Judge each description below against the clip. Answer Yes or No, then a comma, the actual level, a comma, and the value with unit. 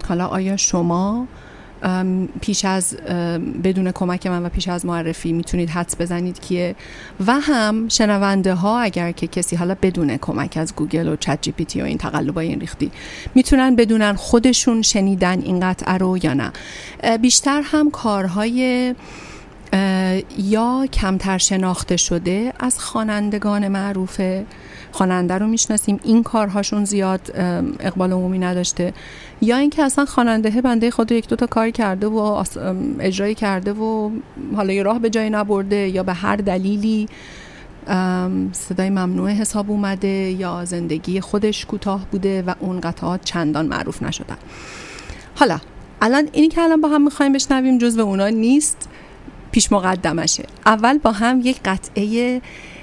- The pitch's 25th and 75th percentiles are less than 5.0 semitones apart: Yes, average, 3.7 semitones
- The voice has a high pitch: Yes, high, 195 Hz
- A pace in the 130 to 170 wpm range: Yes, average, 140 wpm